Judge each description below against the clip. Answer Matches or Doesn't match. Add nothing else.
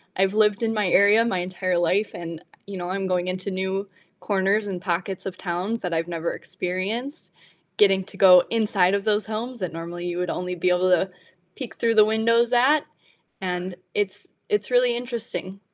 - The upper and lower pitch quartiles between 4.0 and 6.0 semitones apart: Doesn't match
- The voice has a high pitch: Matches